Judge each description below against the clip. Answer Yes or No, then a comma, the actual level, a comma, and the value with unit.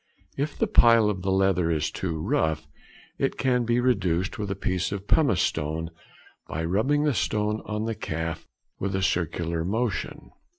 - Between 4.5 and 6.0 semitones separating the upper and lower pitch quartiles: Yes, average, 5.3 semitones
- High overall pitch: No, very low, 95 Hz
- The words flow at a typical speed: Yes, average, 170 wpm